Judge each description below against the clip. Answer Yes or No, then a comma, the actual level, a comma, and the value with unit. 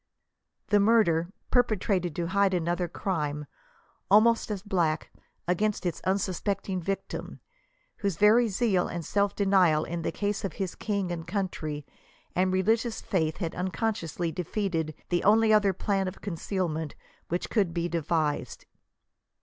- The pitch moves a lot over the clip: No, average, 3.4 semitones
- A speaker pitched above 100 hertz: Yes, medium, 185 Hz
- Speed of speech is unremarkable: Yes, average, 145 wpm